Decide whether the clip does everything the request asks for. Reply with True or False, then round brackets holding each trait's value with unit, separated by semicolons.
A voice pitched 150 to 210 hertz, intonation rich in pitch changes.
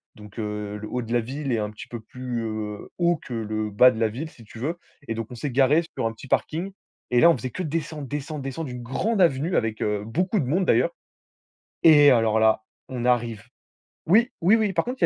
False (125 Hz; 6.1 semitones)